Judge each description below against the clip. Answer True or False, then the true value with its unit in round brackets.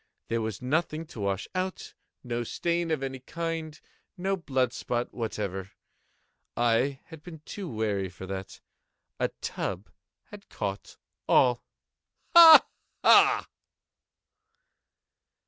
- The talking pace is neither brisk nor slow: False (100 wpm)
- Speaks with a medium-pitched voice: False (130 Hz)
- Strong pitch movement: True (7.2 semitones)